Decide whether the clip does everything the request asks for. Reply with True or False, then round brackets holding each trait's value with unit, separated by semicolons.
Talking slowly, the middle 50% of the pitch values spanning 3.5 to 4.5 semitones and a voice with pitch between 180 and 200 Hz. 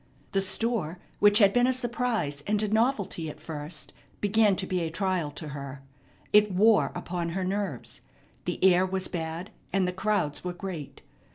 False (175 wpm; 3.9 semitones; 190 Hz)